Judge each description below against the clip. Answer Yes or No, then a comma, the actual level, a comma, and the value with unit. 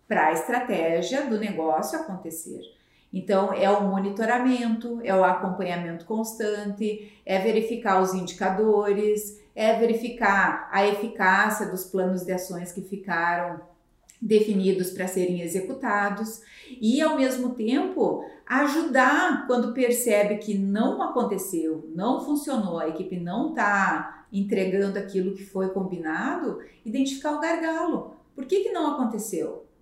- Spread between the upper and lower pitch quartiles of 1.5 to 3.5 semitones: No, average, 4.5 semitones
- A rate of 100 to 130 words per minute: Yes, average, 125 wpm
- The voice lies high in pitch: Yes, high, 210 Hz